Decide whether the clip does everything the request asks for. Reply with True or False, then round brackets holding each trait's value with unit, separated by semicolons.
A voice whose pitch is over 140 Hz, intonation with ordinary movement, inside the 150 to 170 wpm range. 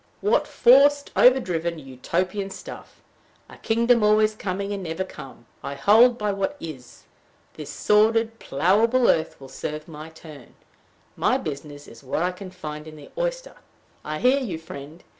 False (185 Hz; 6.8 semitones; 155 wpm)